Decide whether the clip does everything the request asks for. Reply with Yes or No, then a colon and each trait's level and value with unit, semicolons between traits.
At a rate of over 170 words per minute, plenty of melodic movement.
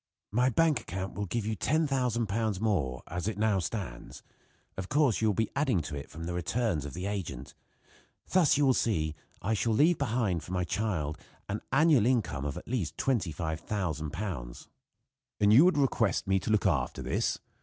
Yes: average, 180 wpm; wide, 6.0 semitones